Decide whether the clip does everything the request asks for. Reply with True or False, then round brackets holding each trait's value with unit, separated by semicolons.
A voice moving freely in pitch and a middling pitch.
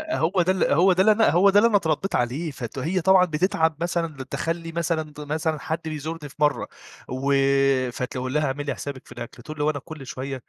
False (3.6 semitones; 155 Hz)